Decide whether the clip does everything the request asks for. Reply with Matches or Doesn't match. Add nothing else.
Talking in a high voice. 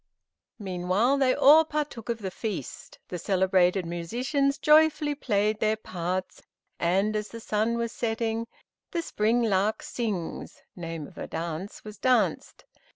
Matches